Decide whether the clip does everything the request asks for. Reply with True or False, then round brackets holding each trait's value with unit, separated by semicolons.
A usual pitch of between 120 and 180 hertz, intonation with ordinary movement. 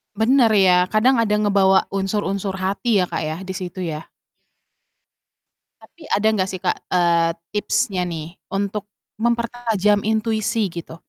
False (200 Hz; 3.0 semitones)